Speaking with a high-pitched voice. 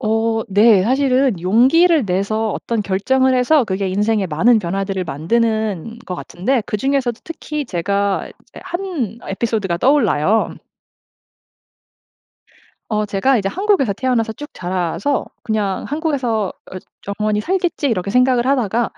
Yes: high, 225 Hz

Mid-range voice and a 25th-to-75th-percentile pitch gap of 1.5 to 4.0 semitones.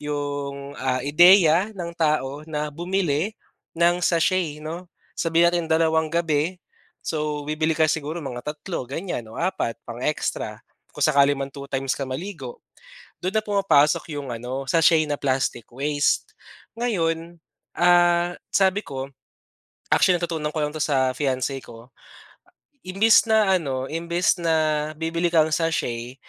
Yes: medium, 155 Hz; average, 3.6 semitones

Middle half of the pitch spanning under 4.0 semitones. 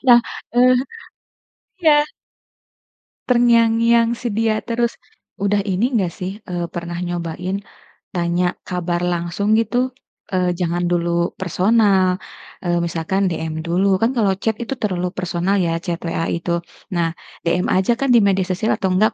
No: average, 4.4 semitones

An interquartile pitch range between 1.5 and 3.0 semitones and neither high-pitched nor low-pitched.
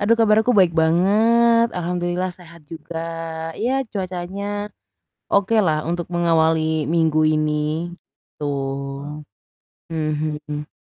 No: average, 4.0 semitones; medium, 175 Hz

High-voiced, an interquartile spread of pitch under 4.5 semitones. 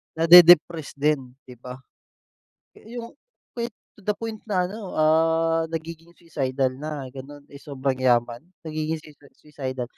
No: medium, 155 Hz; average, 3.9 semitones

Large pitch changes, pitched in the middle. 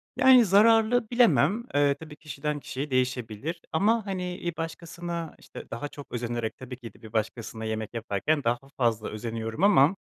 Yes: wide, 7.3 semitones; medium, 145 Hz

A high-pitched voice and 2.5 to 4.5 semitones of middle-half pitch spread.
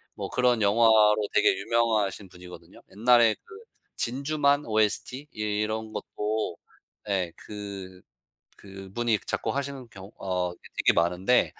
No: low, 105 Hz; average, 3.7 semitones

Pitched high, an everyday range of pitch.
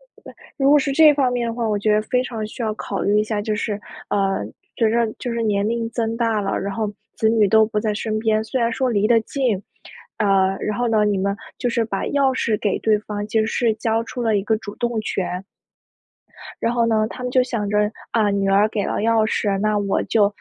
No: high, 220 Hz; narrow, 2.1 semitones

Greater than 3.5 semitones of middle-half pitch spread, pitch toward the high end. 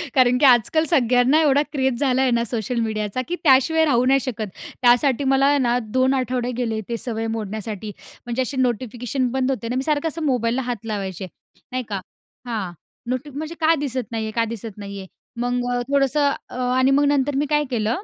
No: average, 3.1 semitones; very high, 250 Hz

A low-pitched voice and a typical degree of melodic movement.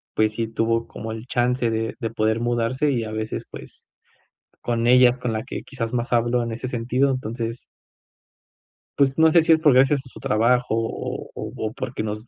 No: low, 120 Hz; narrow, 2.2 semitones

